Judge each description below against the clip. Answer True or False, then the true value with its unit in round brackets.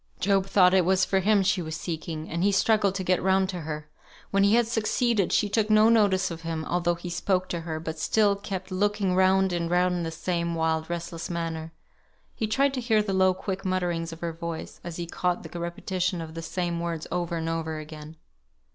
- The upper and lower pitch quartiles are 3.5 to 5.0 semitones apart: False (2.8 semitones)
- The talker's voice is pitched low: False (180 Hz)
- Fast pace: True (220 wpm)